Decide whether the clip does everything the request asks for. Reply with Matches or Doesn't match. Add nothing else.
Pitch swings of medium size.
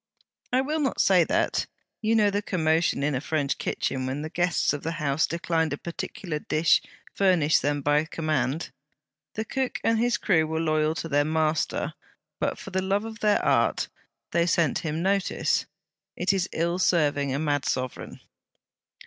Matches